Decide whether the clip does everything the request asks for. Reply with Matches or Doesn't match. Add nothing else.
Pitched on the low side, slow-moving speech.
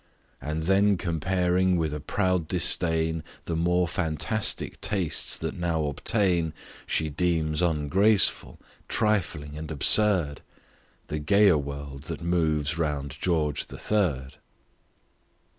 Matches